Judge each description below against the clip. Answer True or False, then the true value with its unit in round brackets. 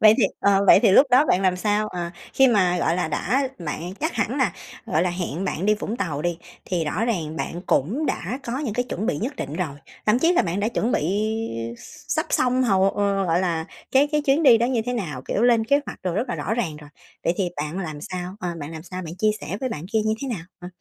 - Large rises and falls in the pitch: True (5.7 semitones)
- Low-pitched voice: False (195 Hz)